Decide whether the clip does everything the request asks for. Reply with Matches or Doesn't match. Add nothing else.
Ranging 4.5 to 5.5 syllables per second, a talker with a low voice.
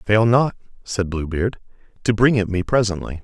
Matches